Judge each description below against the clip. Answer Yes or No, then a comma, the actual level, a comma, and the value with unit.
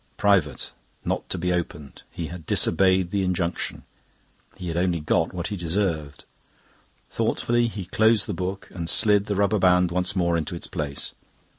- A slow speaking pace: No, average, 165 wpm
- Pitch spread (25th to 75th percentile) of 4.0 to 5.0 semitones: No, average, 2.8 semitones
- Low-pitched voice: Yes, very low, 90 Hz